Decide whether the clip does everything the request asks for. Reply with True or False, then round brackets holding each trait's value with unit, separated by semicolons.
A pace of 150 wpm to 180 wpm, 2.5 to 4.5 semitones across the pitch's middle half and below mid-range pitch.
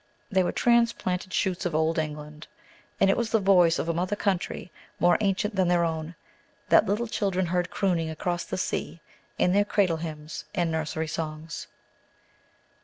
False (170 wpm; 3.2 semitones; 175 Hz)